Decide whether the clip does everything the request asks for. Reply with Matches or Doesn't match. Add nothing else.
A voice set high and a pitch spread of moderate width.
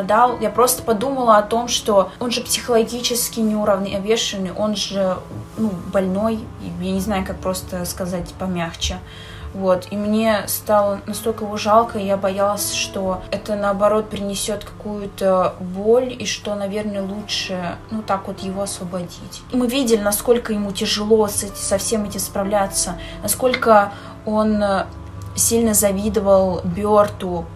Doesn't match